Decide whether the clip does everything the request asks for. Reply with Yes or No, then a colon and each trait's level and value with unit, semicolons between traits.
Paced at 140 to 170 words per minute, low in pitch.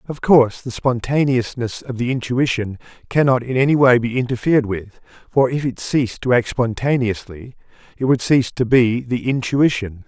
Yes: average, 165 wpm; low, 125 Hz